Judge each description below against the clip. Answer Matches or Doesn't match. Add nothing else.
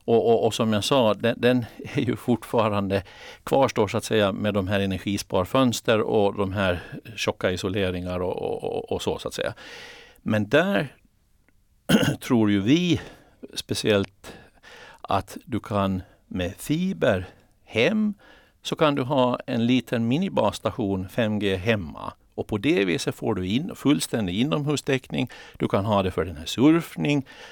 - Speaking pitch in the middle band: Doesn't match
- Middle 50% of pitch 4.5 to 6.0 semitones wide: Matches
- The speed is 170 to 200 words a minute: Doesn't match